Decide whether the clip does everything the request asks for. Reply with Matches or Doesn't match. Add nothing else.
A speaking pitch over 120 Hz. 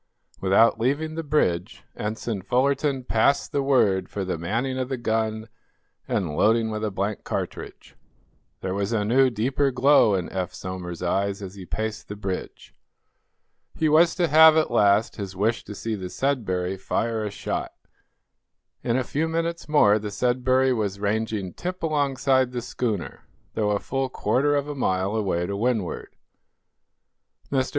Doesn't match